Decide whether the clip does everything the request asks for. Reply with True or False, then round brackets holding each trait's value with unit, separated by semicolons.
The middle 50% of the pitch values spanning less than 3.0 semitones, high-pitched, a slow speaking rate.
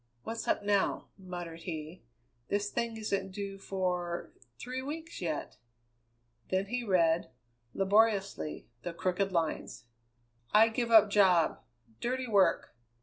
False (3.9 semitones; 195 Hz; 120 wpm)